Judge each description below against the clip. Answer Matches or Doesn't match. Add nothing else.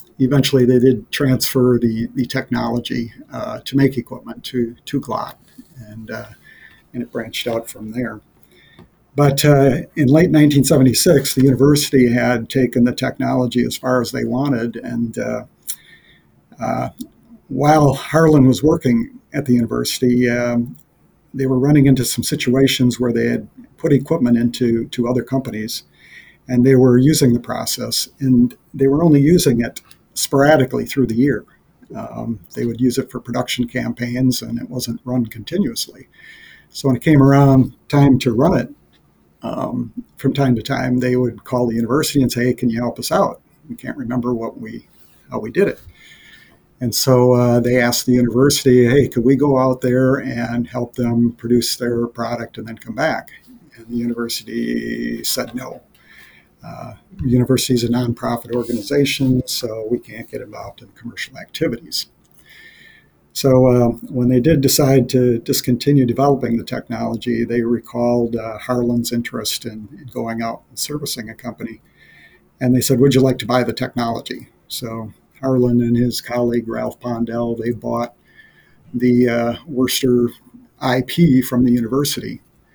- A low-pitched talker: Matches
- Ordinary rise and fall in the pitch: Doesn't match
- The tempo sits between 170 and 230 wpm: Doesn't match